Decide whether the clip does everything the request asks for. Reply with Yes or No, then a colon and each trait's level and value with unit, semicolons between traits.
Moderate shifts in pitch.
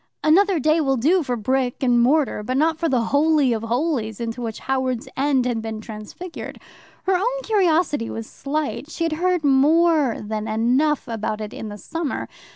No: wide, 5.7 semitones